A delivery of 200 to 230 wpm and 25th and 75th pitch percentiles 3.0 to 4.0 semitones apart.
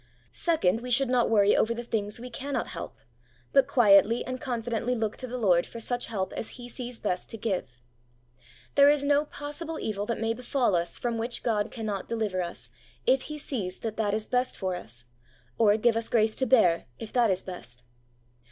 Yes: fast, 205 wpm; average, 3.6 semitones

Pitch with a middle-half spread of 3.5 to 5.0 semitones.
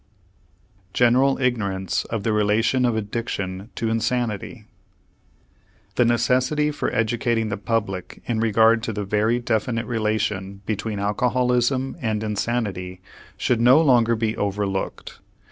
No: average, 2.8 semitones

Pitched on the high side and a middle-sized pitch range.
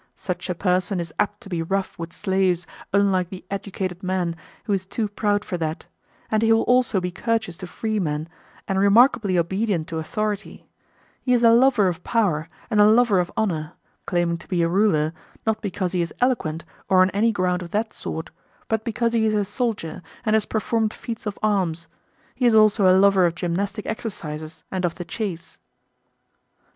Yes: high, 195 Hz; average, 3.6 semitones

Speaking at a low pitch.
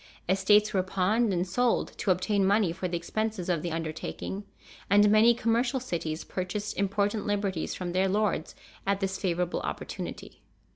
No: high, 195 Hz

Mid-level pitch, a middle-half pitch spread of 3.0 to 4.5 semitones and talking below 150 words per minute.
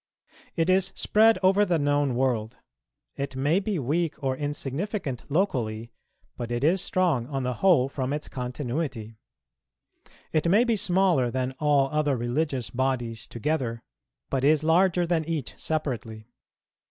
No: medium, 145 Hz; average, 5.2 semitones; average, 140 wpm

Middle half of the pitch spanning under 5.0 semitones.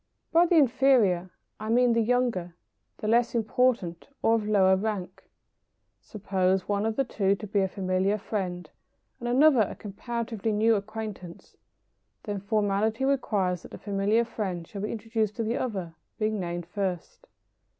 Yes: average, 3.3 semitones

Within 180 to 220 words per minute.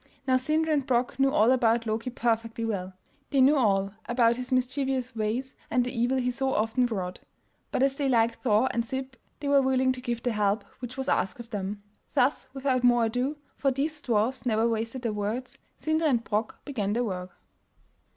Yes: average, 200 wpm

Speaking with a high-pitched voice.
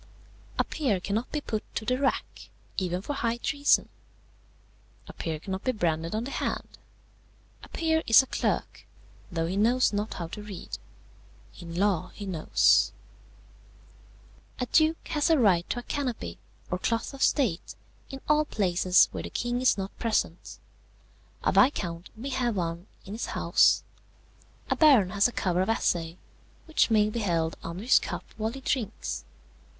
Yes: high, 215 Hz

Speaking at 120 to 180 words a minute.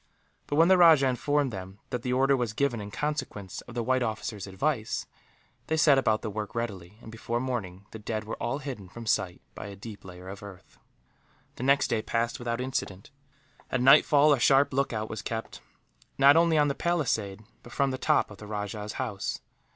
No: average, 200 wpm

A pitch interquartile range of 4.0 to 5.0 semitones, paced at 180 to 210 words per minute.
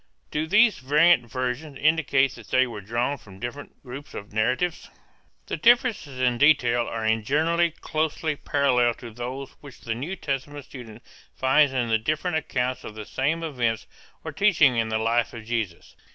No: average, 4.4 semitones; average, 170 wpm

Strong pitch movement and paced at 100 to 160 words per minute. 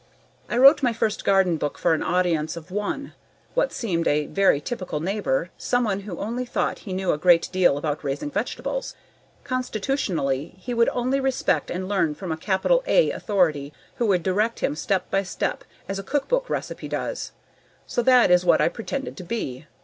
No: wide, 6.3 semitones; average, 185 wpm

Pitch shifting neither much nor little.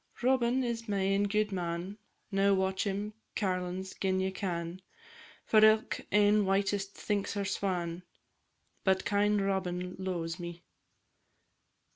No: narrow, 2.1 semitones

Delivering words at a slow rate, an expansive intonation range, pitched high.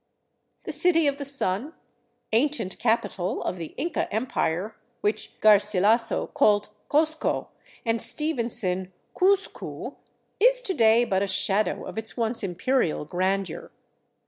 Yes: slow, 120 wpm; wide, 6.5 semitones; high, 220 Hz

